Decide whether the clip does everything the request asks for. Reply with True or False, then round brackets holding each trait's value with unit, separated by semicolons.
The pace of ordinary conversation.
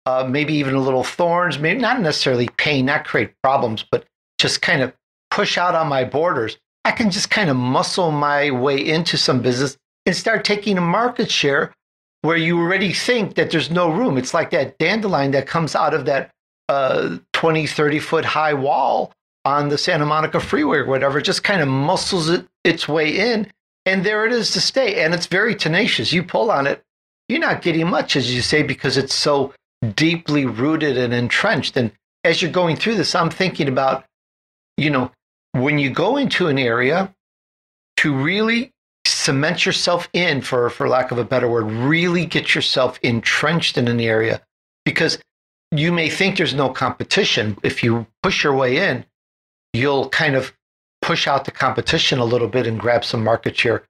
True (190 wpm)